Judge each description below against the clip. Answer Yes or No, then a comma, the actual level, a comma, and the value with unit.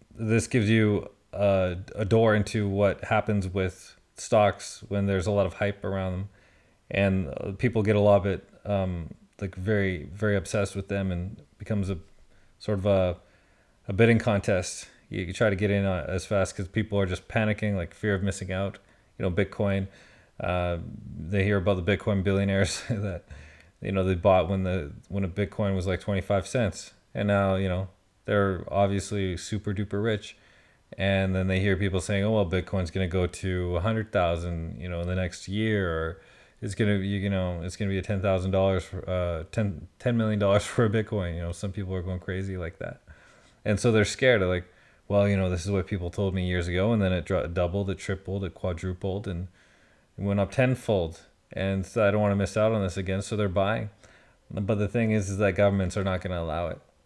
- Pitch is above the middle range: No, low, 100 Hz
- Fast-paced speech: Yes, fast, 210 wpm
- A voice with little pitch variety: Yes, narrow, 1.9 semitones